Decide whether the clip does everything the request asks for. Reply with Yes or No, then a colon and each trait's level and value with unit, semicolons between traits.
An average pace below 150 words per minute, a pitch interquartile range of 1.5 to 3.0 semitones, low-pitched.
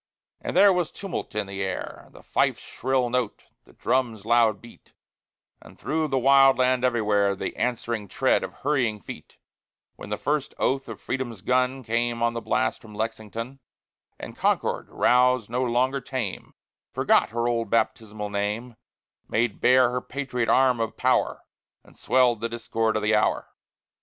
No: average, 160 wpm; average, 2.7 semitones; low, 120 Hz